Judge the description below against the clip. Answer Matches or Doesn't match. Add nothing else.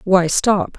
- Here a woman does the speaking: Matches